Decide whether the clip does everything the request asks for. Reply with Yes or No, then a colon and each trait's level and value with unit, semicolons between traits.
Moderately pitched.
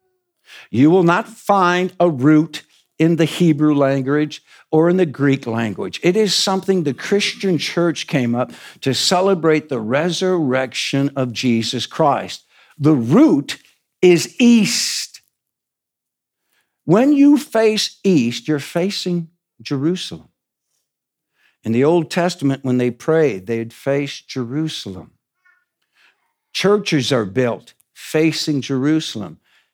Yes: medium, 160 Hz